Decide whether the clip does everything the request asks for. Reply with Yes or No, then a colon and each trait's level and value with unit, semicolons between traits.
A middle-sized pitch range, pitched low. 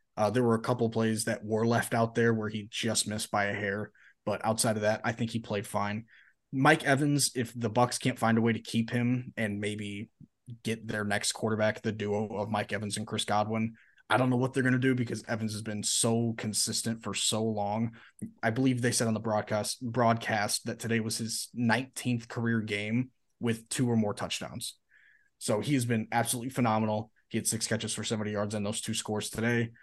No: narrow, 1.8 semitones; low, 115 Hz